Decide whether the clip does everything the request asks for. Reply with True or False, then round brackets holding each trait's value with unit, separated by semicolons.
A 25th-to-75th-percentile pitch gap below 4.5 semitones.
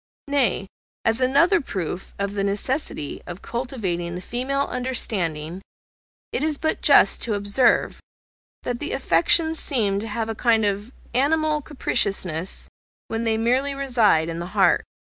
False (5.4 semitones)